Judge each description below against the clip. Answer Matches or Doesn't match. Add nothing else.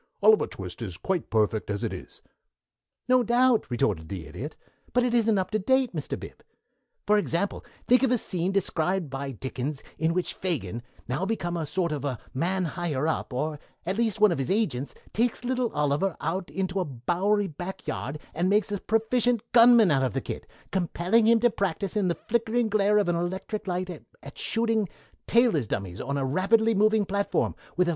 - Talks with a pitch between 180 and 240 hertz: Matches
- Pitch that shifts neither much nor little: Doesn't match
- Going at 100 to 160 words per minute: Doesn't match